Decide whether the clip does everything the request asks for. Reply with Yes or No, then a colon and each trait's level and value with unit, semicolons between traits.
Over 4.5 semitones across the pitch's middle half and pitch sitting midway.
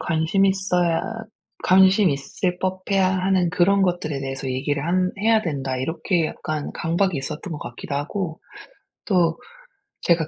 No: average, 3.9 semitones; medium, 175 Hz